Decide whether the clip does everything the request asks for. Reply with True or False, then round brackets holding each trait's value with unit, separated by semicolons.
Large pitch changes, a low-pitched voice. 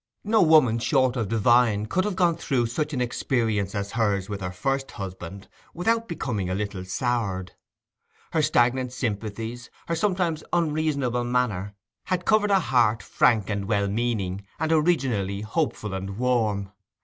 True (6.8 semitones; 120 Hz)